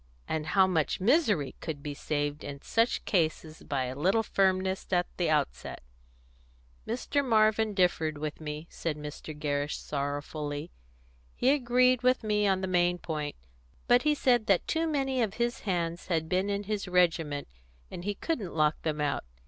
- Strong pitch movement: Yes, wide, 6.2 semitones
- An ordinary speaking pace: Yes, average, 165 wpm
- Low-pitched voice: No, medium, 180 Hz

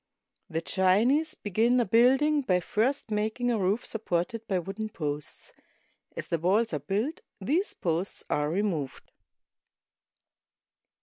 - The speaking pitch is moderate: No, high, 210 Hz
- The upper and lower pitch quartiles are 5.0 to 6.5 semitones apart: Yes, average, 5.3 semitones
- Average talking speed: No, slow, 125 wpm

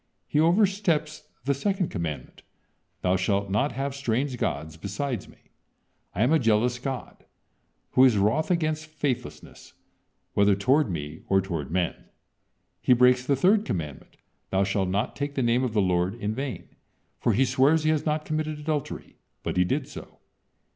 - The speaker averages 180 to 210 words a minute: No, average, 165 wpm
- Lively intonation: Yes, wide, 7.4 semitones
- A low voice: Yes, low, 125 Hz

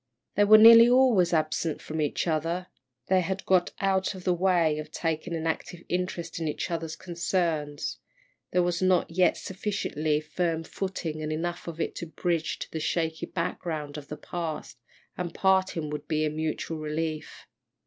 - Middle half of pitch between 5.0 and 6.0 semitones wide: No, average, 2.8 semitones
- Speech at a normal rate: Yes, average, 170 wpm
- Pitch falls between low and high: Yes, medium, 170 Hz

